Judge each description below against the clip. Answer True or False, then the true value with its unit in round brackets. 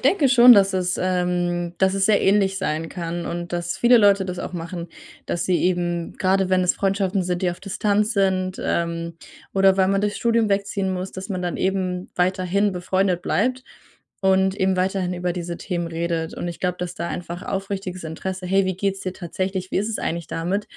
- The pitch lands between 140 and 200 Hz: True (185 Hz)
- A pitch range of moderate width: False (1.8 semitones)